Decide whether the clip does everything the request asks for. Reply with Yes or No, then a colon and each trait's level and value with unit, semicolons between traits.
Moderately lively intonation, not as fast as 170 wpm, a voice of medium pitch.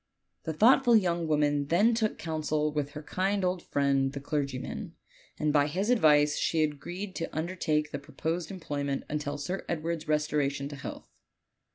Yes: average, 3.4 semitones; average, 160 wpm; medium, 155 Hz